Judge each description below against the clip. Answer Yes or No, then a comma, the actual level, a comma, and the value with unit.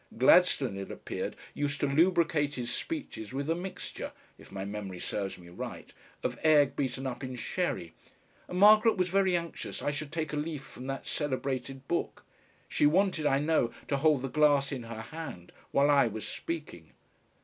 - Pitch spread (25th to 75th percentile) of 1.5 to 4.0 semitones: No, average, 4.5 semitones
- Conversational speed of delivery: Yes, average, 180 wpm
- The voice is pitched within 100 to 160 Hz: Yes, medium, 140 Hz